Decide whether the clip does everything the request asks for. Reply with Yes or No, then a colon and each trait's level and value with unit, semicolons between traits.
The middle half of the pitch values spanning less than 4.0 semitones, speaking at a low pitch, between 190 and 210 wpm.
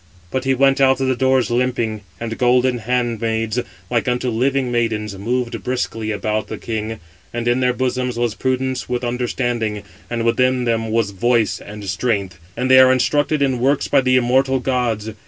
No: narrow, 2.4 semitones; low, 120 Hz; average, 175 wpm